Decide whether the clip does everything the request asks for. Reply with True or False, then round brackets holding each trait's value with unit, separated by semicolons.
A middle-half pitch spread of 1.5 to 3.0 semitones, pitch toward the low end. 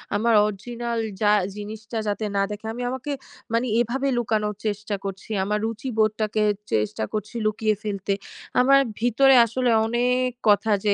False (2.4 semitones; 220 Hz)